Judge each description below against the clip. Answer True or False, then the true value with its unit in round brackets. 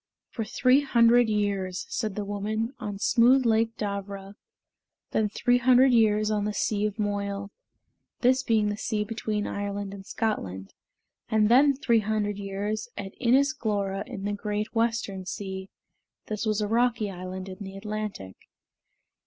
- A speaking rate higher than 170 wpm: False (155 wpm)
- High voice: True (210 Hz)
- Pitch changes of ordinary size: False (2.3 semitones)